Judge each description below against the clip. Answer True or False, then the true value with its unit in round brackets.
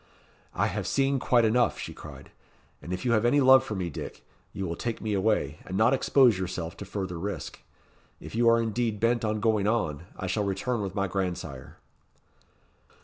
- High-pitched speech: False (105 Hz)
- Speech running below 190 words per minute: False (195 wpm)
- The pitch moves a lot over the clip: False (3.9 semitones)